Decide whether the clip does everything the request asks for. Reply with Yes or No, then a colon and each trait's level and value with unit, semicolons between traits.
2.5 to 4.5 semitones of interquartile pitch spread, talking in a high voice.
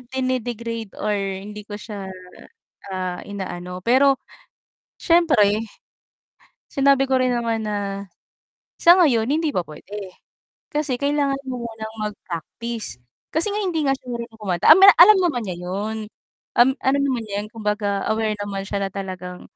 No: average, 5.0 semitones; high, 225 Hz